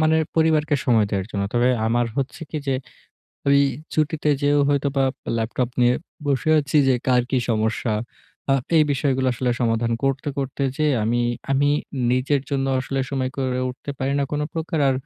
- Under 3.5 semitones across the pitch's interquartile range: Yes, average, 2.8 semitones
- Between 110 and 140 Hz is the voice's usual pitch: Yes, low, 135 Hz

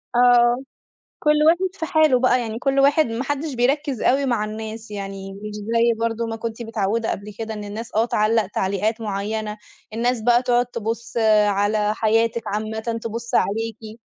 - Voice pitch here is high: Yes, high, 225 Hz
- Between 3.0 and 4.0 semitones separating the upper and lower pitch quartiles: No, narrow, 2.4 semitones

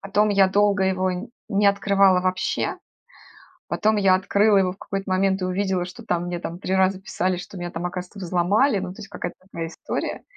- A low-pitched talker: No, high, 190 Hz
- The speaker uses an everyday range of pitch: No, narrow, 1.6 semitones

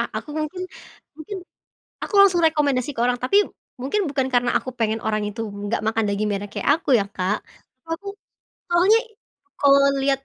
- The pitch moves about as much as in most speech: No, wide, 6.6 semitones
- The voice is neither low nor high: No, very high, 265 Hz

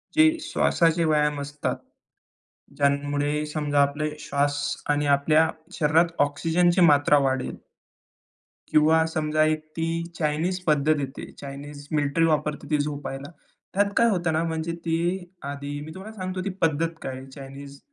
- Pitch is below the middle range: No, medium, 150 Hz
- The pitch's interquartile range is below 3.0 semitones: Yes, narrow, 2.4 semitones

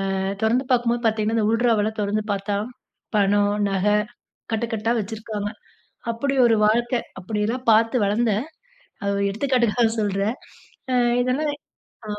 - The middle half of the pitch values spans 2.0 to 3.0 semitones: Yes, narrow, 2.4 semitones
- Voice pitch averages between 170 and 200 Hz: No, high, 220 Hz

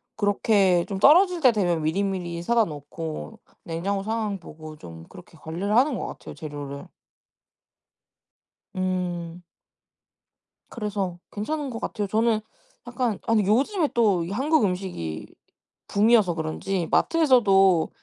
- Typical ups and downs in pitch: Yes, average, 4.9 semitones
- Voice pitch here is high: Yes, high, 195 Hz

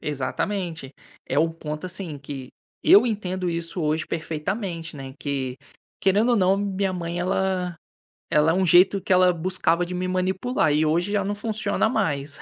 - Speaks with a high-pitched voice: No, medium, 180 Hz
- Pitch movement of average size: Yes, average, 3.7 semitones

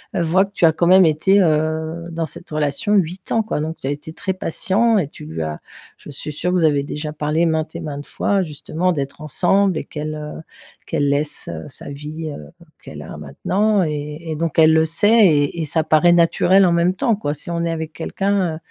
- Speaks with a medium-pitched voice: Yes, medium, 160 Hz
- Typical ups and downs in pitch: Yes, average, 3.2 semitones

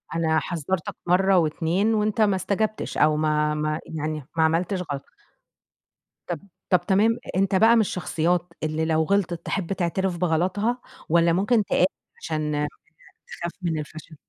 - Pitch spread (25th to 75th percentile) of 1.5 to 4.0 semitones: Yes, average, 3.6 semitones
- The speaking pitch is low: No, medium, 170 Hz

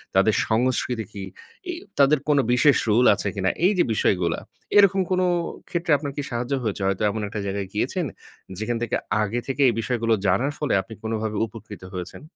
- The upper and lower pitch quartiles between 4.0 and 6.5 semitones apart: Yes, average, 5.2 semitones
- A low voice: Yes, low, 115 Hz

